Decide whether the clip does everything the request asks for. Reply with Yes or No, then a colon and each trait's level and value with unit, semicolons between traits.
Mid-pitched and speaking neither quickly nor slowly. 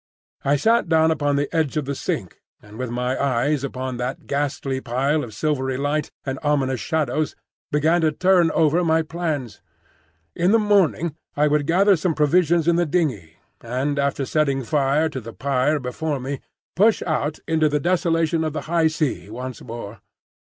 Yes: medium, 150 Hz; average, 175 wpm